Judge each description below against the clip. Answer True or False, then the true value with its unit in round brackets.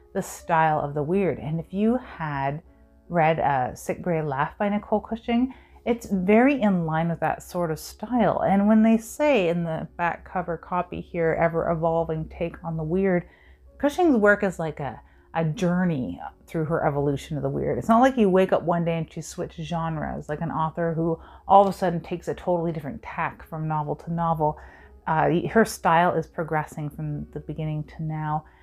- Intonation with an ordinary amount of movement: True (3.5 semitones)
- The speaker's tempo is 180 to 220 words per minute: True (195 wpm)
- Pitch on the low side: False (165 Hz)